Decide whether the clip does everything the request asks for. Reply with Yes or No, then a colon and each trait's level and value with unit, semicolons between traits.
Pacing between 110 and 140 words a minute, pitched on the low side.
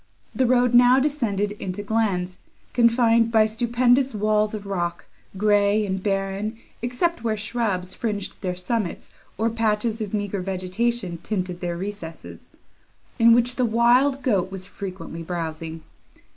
No: slow, 135 wpm; high, 210 Hz